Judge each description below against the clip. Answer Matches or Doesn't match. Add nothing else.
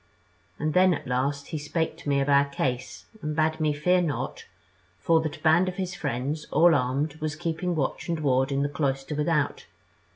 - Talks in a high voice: Doesn't match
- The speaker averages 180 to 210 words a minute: Matches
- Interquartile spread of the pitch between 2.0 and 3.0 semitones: Matches